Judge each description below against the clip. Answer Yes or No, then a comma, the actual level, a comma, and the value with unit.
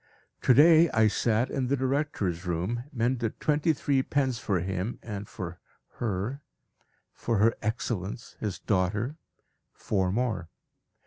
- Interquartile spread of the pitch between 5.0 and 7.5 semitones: Yes, wide, 5.4 semitones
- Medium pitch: No, low, 115 Hz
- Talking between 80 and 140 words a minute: Yes, slow, 135 wpm